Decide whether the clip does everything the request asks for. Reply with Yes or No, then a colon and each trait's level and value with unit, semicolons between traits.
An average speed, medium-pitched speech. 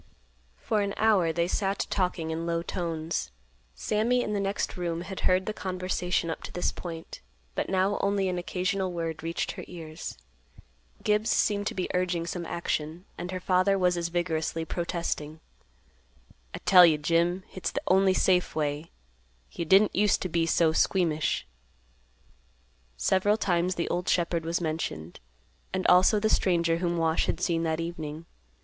Yes: average, 165 wpm; medium, 175 Hz